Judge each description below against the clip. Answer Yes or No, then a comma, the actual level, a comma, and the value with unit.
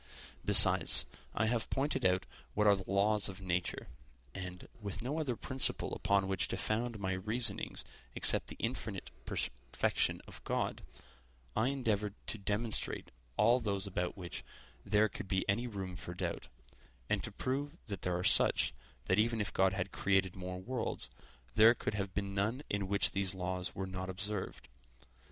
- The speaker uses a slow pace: No, average, 165 wpm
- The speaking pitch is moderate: No, low, 100 Hz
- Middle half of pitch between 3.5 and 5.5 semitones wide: No, average, 2.9 semitones